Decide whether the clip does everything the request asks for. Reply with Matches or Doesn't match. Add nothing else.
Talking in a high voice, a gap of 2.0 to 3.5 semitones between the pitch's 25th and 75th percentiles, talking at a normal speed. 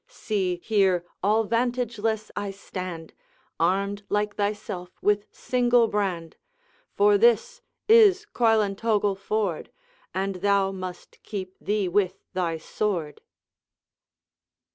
Doesn't match